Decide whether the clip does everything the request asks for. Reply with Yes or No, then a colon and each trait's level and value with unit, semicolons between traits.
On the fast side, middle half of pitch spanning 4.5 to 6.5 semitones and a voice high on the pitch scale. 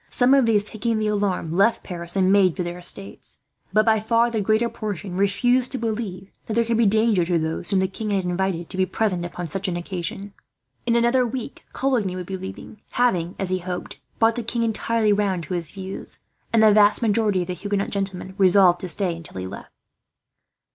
No: fast, 215 wpm; average, 3.5 semitones; high, 200 Hz